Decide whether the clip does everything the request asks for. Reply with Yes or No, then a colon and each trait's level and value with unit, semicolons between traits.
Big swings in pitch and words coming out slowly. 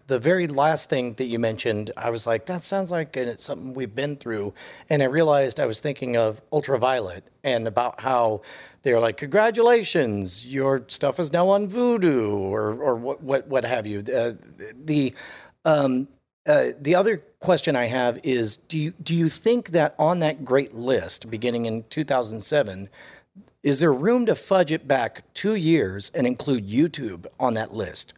No: wide, 5.7 semitones; average, 175 wpm